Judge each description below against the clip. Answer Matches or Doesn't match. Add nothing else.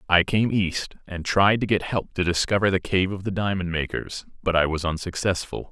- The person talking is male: Matches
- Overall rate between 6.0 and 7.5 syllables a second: Doesn't match